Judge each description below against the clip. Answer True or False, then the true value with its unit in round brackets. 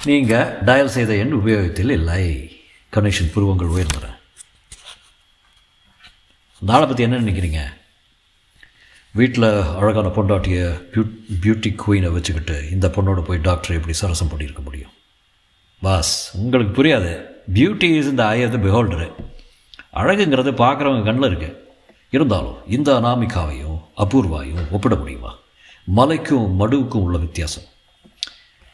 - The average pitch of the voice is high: False (95 Hz)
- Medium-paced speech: True (105 wpm)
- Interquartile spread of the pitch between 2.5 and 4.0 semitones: False (5.2 semitones)